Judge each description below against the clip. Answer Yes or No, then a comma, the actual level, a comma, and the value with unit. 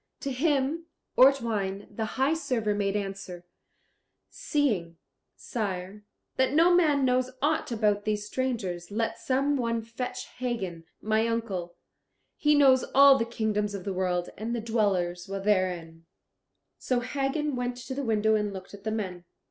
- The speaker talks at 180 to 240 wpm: No, average, 150 wpm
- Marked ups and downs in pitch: No, average, 4.9 semitones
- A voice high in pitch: Yes, high, 220 Hz